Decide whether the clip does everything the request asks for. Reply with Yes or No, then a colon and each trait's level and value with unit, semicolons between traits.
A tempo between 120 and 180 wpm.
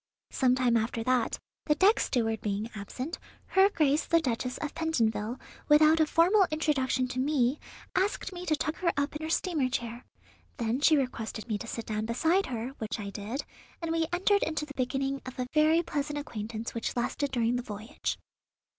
No: average, 190 wpm